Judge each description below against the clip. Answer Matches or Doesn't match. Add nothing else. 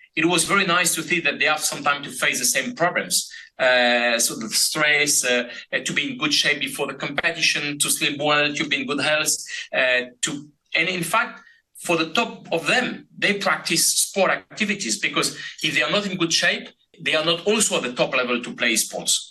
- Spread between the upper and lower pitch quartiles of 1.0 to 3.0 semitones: Doesn't match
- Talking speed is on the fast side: Matches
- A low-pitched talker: Doesn't match